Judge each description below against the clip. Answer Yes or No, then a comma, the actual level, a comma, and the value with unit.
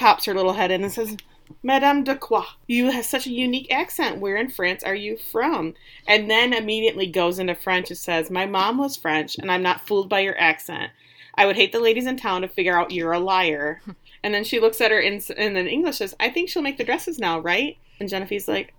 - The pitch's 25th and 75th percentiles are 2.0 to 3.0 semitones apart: No, average, 4.1 semitones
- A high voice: Yes, high, 200 Hz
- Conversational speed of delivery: No, fast, 245 wpm